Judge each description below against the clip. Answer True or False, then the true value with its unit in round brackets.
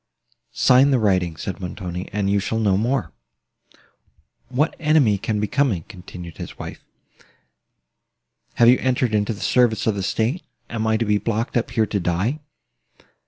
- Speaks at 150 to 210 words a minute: True (165 wpm)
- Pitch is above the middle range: False (110 Hz)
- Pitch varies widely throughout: False (4.0 semitones)